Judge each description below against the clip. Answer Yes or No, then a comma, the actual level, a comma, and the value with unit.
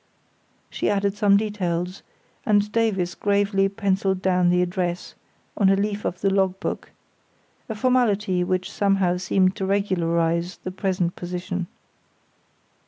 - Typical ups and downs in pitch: No, narrow, 2.1 semitones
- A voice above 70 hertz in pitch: Yes, high, 190 Hz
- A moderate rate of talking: No, slow, 130 wpm